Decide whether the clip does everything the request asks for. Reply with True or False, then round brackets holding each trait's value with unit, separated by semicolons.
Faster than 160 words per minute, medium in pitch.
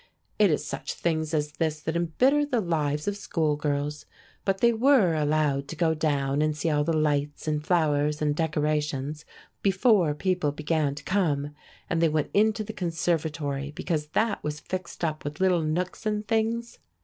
True (175 wpm; 155 Hz)